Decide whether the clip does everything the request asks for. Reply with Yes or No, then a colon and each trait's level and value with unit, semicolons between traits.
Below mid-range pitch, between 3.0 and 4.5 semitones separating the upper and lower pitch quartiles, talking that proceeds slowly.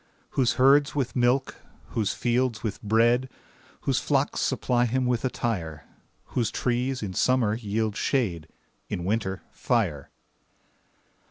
Yes: low, 120 Hz; average, 3.5 semitones; slow, 120 wpm